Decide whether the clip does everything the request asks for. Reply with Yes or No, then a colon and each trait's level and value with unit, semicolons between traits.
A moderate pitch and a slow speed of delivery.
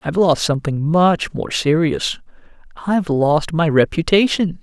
Yes: medium, 165 Hz; slow, 130 wpm